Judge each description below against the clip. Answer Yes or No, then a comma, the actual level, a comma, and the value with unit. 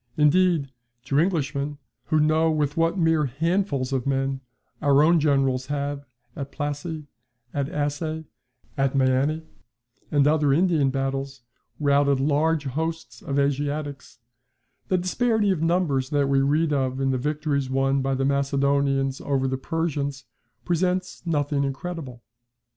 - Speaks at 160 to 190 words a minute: No, slow, 135 wpm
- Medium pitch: Yes, medium, 145 Hz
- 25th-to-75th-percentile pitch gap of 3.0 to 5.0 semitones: No, narrow, 2.6 semitones